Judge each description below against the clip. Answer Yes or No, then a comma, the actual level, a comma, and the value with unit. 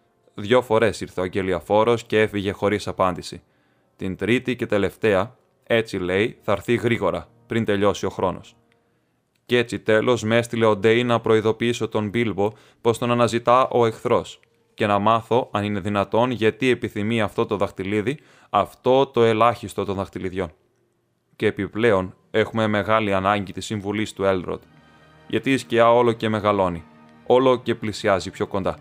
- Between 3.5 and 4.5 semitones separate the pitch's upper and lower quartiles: No, average, 2.9 semitones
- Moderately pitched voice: No, low, 110 Hz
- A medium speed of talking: Yes, average, 155 wpm